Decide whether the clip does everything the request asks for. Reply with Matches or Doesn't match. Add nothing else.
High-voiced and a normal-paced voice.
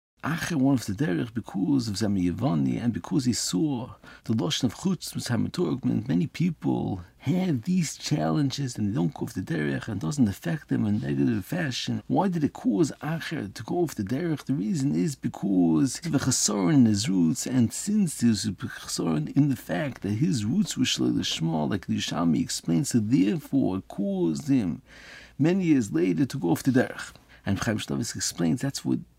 Doesn't match